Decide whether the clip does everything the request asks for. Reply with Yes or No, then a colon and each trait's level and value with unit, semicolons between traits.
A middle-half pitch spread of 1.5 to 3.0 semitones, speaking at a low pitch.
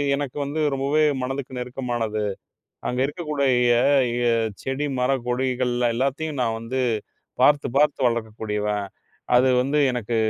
Yes: average, 2.7 semitones; low, 130 Hz